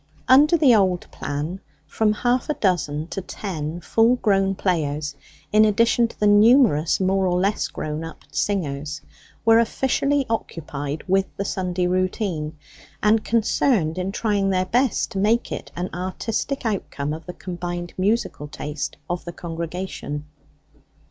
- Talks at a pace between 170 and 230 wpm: No, average, 145 wpm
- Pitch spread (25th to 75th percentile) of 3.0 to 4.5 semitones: No, average, 5.1 semitones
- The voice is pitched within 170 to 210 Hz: Yes, high, 190 Hz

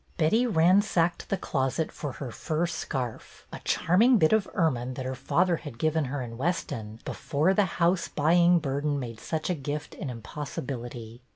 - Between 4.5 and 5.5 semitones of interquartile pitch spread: Yes, average, 5.1 semitones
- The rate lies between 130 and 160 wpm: No, average, 170 wpm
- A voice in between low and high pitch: Yes, medium, 155 Hz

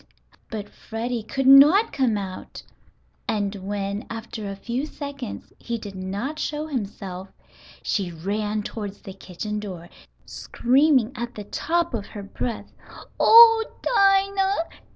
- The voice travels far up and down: Yes, wide, 6.0 semitones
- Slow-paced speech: Yes, slow, 130 wpm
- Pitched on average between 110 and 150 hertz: No, high, 225 Hz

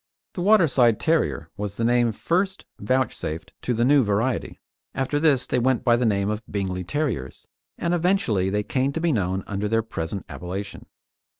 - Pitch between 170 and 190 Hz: No, low, 115 Hz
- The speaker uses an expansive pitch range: Yes, wide, 6.2 semitones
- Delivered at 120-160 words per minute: No, average, 175 wpm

